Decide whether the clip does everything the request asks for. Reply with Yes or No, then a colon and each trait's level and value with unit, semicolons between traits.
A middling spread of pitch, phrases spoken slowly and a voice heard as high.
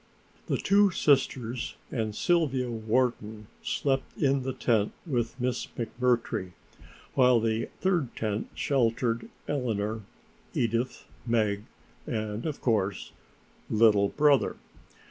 No: average, 3.3 semitones; slow, 105 wpm; low, 120 Hz